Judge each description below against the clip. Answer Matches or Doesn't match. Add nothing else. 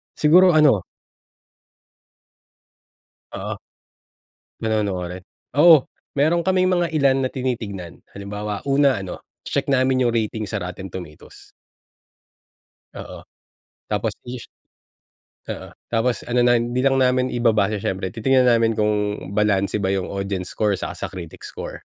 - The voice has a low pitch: Matches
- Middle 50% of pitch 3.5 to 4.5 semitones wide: Doesn't match